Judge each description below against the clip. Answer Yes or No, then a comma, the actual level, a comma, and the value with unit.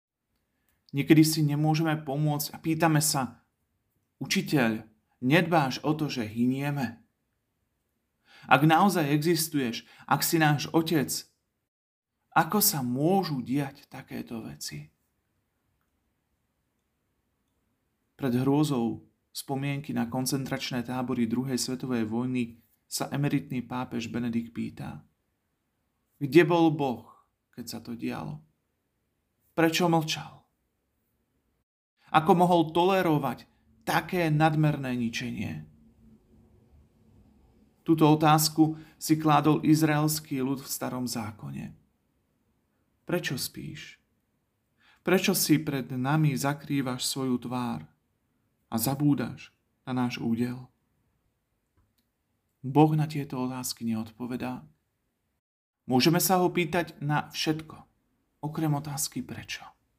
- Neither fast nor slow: No, slow, 90 wpm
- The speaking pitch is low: Yes, low, 130 Hz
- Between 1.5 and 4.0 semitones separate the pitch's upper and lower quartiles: No, average, 5.0 semitones